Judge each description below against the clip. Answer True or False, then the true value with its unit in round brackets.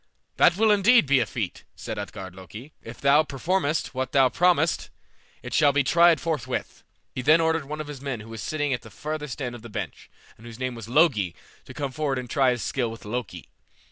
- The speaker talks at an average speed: False (225 wpm)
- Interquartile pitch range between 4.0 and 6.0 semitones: True (4.7 semitones)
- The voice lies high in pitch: False (135 Hz)